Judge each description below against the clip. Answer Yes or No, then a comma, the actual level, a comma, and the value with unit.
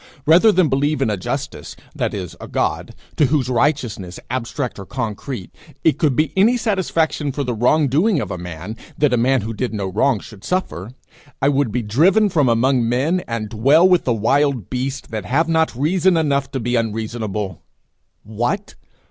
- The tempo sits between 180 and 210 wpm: Yes, average, 185 wpm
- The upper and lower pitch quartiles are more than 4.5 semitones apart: Yes, wide, 5.5 semitones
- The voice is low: Yes, low, 130 Hz